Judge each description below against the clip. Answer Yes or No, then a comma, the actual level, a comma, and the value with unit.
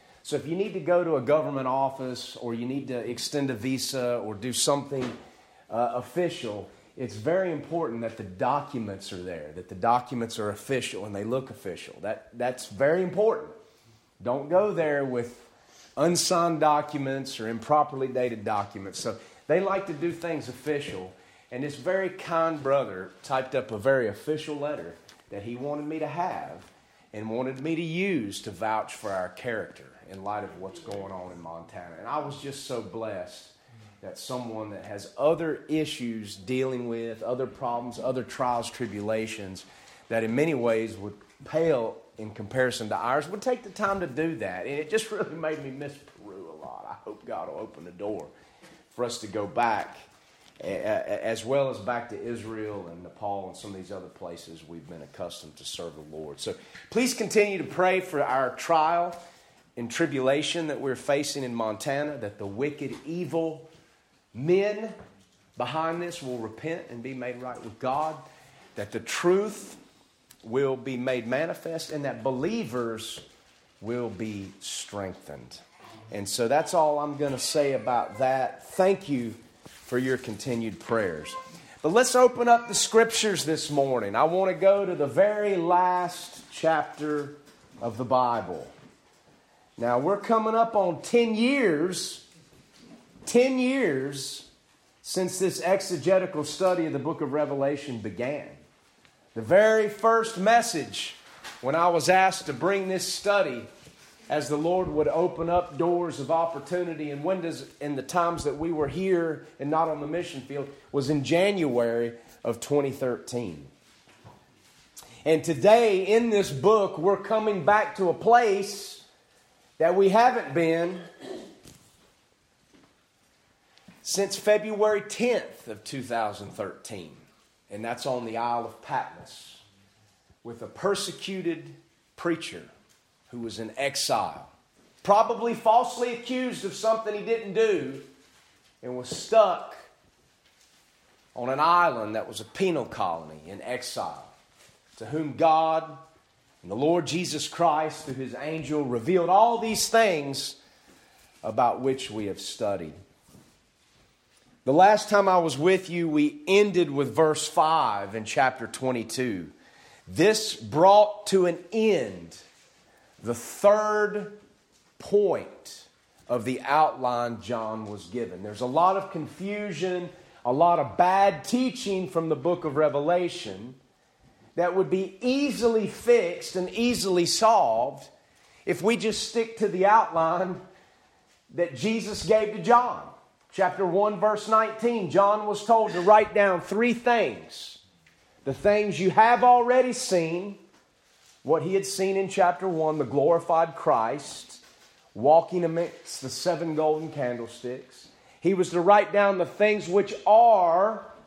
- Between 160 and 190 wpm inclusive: No, average, 145 wpm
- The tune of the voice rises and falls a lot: Yes, wide, 7.5 semitones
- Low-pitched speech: No, medium, 155 Hz